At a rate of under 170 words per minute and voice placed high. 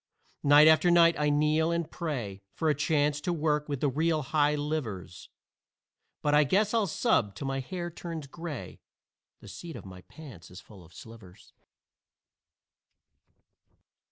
No: average, 155 wpm; medium, 150 Hz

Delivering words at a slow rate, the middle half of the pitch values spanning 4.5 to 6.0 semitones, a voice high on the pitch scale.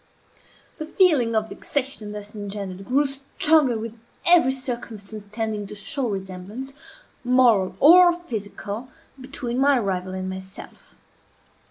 Yes: slow, 120 wpm; average, 5.1 semitones; high, 230 Hz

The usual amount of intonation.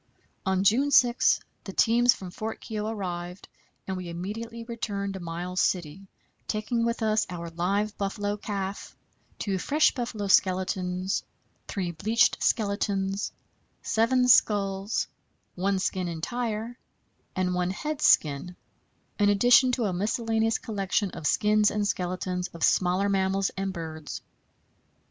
Yes: average, 3.4 semitones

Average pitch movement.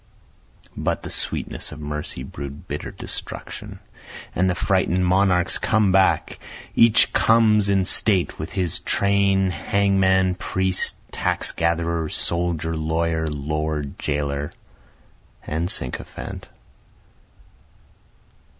Yes: average, 3.8 semitones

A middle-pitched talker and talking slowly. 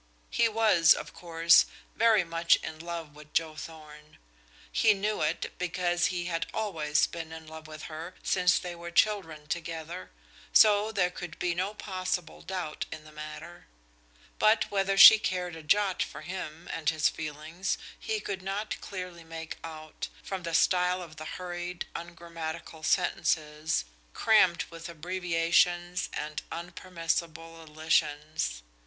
No: medium, 170 Hz; average, 145 wpm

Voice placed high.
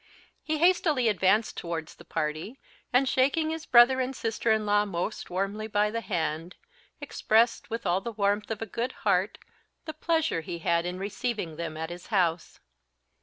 Yes: high, 210 Hz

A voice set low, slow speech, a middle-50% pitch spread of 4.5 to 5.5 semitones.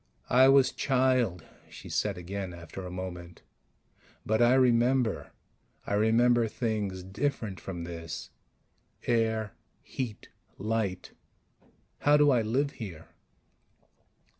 Yes: low, 110 Hz; slow, 110 wpm; average, 5.2 semitones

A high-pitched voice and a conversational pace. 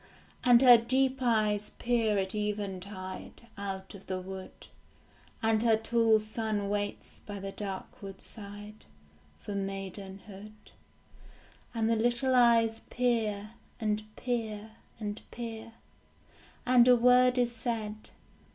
No: high, 215 Hz; slow, 115 wpm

